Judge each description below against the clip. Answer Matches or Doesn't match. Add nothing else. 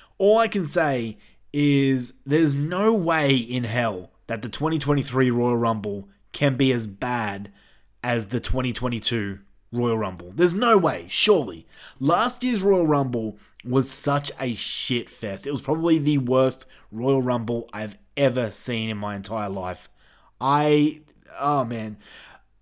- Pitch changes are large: Doesn't match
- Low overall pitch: Matches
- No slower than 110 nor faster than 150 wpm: Matches